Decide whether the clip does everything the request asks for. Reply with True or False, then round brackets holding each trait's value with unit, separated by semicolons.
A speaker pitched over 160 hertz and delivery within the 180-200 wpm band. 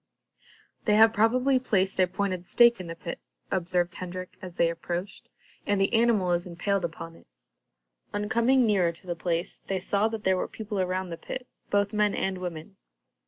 True (190 Hz; 185 wpm)